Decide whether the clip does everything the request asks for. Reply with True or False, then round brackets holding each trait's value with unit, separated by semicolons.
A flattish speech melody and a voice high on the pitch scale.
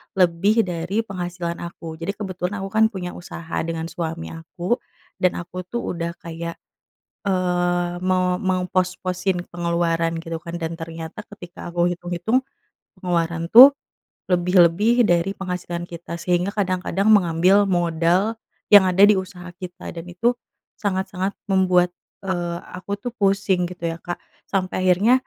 False (2.1 semitones; 180 Hz)